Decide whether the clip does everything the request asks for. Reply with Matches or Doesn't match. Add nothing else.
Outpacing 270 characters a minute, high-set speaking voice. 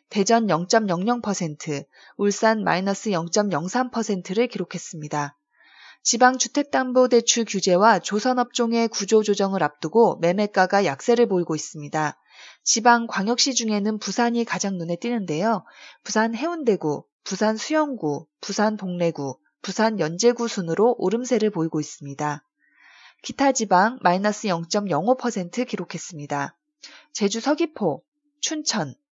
Doesn't match